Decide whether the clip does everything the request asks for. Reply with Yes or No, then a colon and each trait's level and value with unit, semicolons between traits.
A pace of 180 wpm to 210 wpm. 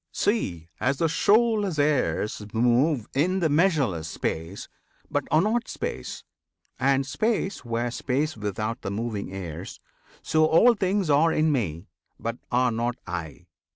No: average, 140 wpm